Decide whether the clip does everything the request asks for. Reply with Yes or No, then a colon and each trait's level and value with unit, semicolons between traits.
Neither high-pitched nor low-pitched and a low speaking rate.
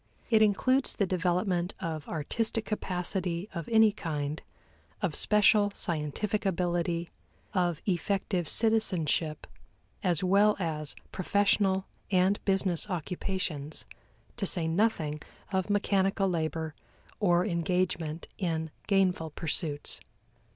Yes: medium, 180 Hz; slow, 100 wpm